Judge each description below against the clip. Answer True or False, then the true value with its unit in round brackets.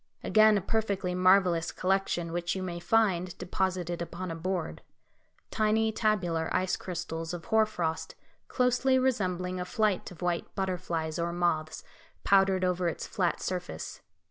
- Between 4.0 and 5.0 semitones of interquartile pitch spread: False (2.5 semitones)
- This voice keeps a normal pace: True (145 wpm)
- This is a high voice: False (180 Hz)